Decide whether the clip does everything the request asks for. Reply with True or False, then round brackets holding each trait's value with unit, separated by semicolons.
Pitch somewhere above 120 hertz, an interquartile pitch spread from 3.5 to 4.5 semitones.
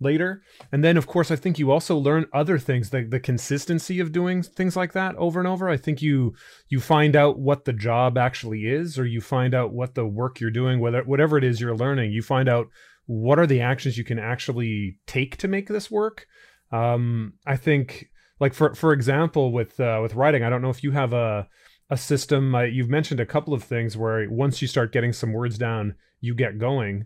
True (135 Hz; 4.1 semitones)